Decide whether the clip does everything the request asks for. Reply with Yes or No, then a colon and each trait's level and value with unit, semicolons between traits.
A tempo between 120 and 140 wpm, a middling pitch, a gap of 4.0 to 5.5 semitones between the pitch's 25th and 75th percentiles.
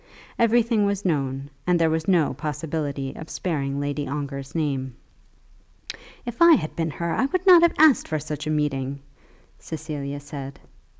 No: average, 160 wpm; medium, 155 Hz; average, 4.3 semitones